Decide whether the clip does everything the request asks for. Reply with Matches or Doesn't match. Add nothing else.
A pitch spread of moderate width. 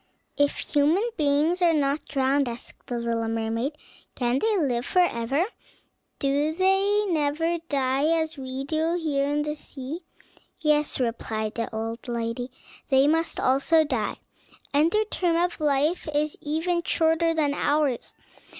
Matches